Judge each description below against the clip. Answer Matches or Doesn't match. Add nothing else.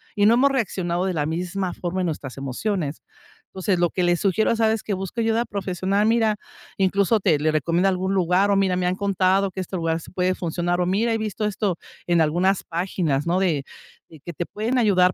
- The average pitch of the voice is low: Doesn't match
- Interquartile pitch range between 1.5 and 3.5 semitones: Matches